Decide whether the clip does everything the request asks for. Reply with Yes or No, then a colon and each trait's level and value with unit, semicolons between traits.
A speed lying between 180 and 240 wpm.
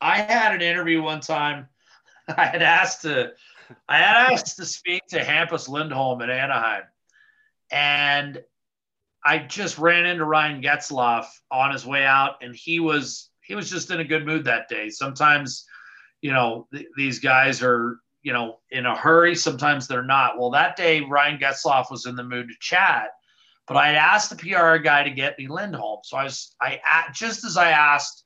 Yes: average, 185 wpm